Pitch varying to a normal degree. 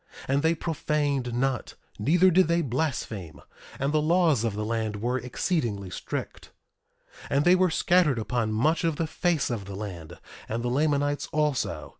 No: wide, 6.0 semitones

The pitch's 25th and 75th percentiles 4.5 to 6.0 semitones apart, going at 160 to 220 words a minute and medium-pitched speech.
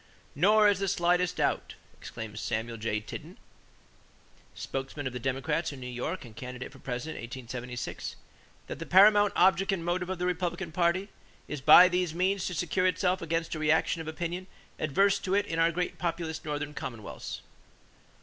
Yes: wide, 5.5 semitones; average, 180 wpm; medium, 165 Hz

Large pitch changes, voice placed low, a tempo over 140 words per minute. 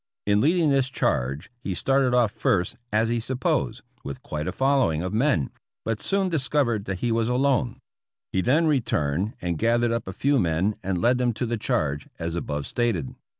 Yes: wide, 6.6 semitones; low, 115 Hz; average, 195 wpm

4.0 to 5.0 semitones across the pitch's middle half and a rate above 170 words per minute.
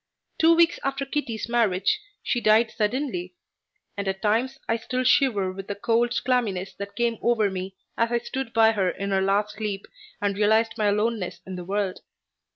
No: average, 3.3 semitones; average, 180 wpm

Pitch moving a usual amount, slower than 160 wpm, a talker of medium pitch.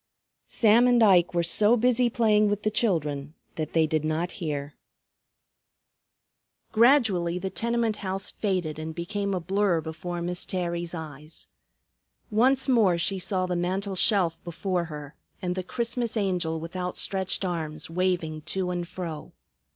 Yes: average, 4.0 semitones; average, 145 wpm; medium, 180 Hz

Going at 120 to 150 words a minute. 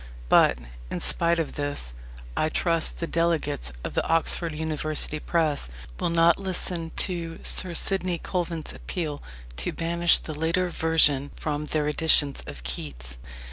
Yes: average, 140 wpm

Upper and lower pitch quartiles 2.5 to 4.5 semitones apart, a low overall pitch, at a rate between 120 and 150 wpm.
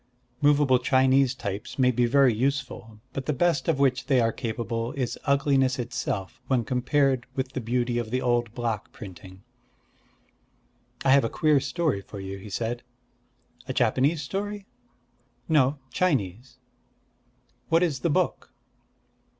Yes: average, 3.1 semitones; low, 130 Hz; average, 140 wpm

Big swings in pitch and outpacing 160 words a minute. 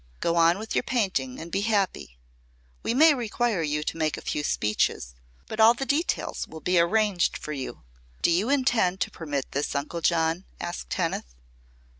Yes: wide, 6.2 semitones; average, 180 wpm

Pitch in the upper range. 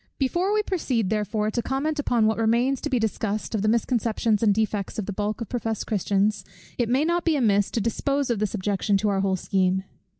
Yes: high, 220 Hz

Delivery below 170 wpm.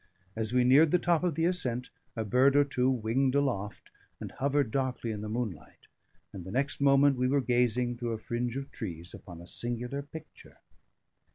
No: average, 190 wpm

